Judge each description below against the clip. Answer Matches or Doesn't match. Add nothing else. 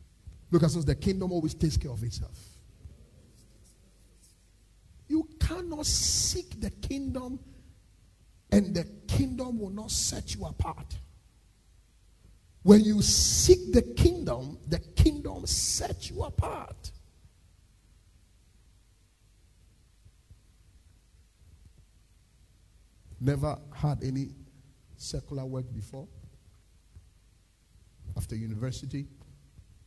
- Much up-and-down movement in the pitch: Matches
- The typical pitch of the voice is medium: Doesn't match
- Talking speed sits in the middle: Doesn't match